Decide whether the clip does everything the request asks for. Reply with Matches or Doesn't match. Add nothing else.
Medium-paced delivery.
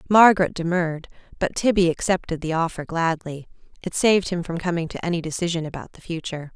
Matches